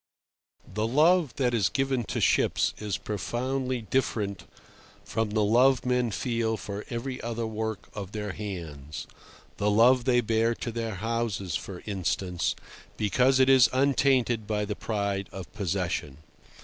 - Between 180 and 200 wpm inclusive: No, slow, 135 wpm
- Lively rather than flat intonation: No, average, 3.7 semitones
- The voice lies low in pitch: Yes, low, 110 Hz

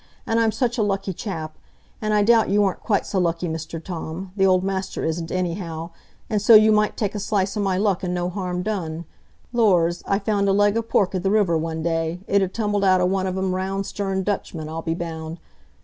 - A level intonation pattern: No, average, 3.2 semitones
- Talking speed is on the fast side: Yes, fast, 225 wpm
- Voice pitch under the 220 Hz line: Yes, high, 190 Hz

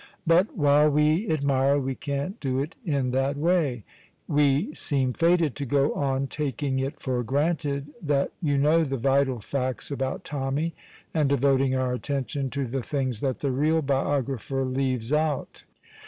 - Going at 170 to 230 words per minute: No, average, 155 wpm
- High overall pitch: No, medium, 140 Hz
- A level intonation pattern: Yes, narrow, 2.1 semitones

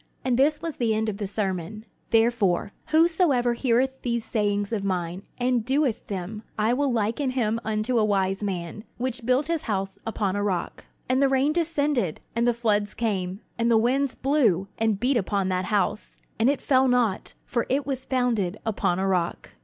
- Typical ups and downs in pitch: Yes, average, 4.4 semitones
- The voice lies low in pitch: No, high, 225 Hz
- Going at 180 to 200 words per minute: Yes, average, 185 wpm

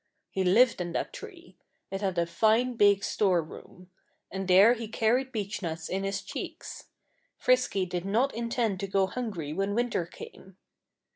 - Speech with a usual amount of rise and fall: Yes, average, 4.1 semitones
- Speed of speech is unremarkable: Yes, average, 155 wpm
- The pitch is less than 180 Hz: No, high, 195 Hz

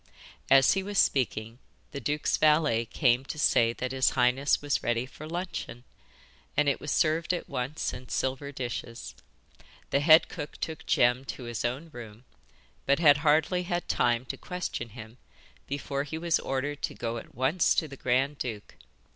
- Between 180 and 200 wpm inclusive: No, average, 170 wpm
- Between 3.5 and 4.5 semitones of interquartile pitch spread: Yes, average, 3.9 semitones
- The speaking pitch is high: No, low, 135 Hz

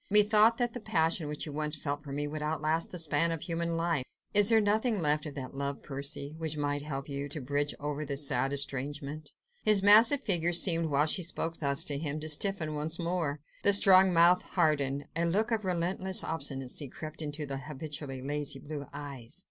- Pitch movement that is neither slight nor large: Yes, average, 3.4 semitones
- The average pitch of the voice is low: No, medium, 155 Hz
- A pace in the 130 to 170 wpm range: No, average, 200 wpm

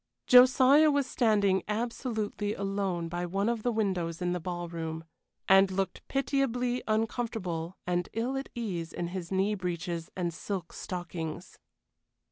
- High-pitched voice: Yes, high, 195 Hz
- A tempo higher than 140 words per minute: No, slow, 135 wpm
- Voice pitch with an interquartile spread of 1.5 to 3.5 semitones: No, average, 4.7 semitones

